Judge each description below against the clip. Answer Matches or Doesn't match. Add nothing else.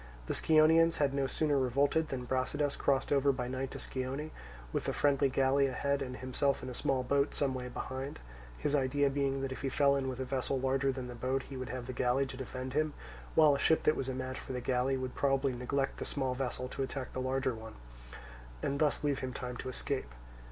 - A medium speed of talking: Doesn't match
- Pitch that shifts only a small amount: Matches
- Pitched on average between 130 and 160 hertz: Matches